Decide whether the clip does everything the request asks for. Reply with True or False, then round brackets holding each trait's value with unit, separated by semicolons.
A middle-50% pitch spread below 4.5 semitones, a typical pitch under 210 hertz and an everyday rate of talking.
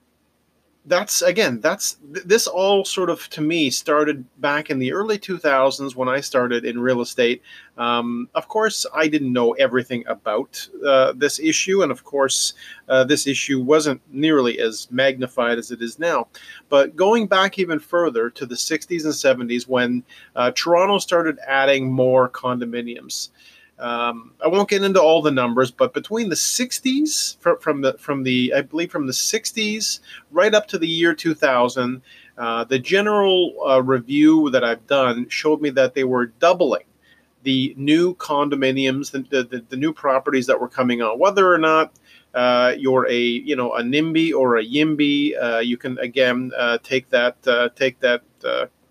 False (4.8 semitones; 140 Hz; 180 wpm)